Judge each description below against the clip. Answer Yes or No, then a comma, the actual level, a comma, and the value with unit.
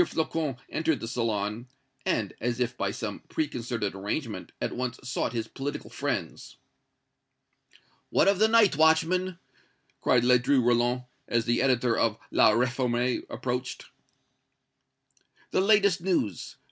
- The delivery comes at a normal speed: No, slow, 125 wpm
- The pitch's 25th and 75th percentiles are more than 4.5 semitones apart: Yes, average, 5.2 semitones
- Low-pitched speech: Yes, low, 125 Hz